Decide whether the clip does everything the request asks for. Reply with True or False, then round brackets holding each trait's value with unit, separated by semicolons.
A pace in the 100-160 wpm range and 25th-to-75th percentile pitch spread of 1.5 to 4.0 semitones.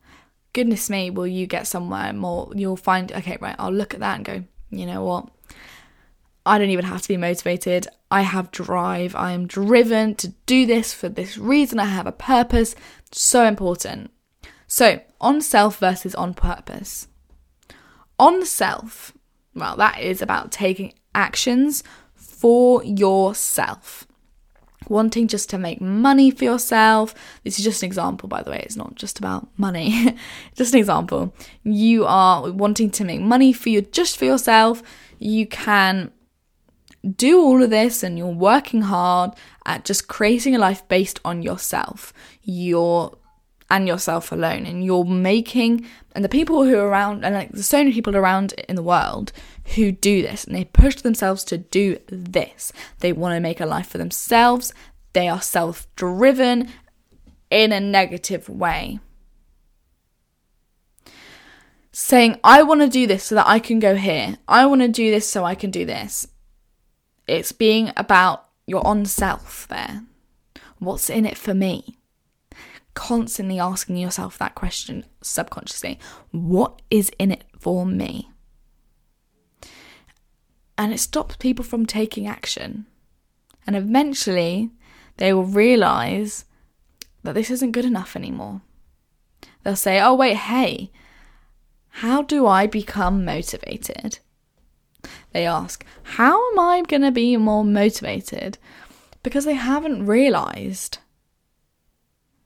False (145 wpm; 4.5 semitones)